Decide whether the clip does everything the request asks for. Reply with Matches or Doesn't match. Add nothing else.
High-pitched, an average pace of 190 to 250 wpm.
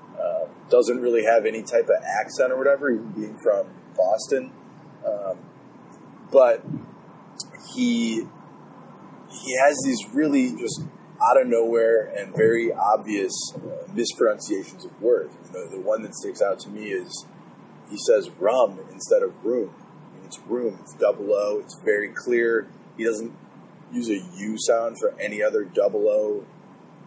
Doesn't match